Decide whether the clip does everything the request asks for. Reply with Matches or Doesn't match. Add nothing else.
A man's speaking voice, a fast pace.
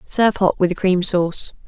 Doesn't match